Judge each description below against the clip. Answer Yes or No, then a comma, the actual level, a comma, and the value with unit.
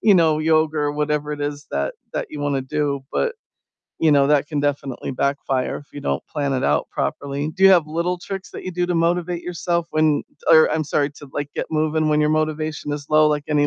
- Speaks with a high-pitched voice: No, medium, 150 Hz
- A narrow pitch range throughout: Yes, narrow, 1.8 semitones